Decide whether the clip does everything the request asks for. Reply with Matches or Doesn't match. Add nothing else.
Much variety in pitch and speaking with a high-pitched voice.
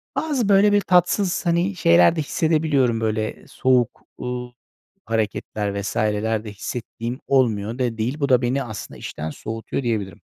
Doesn't match